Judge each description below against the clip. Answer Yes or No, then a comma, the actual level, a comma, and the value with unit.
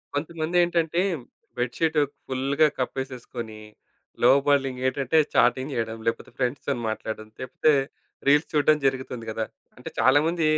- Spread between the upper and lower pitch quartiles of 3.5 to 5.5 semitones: Yes, average, 3.9 semitones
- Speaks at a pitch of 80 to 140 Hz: Yes, low, 135 Hz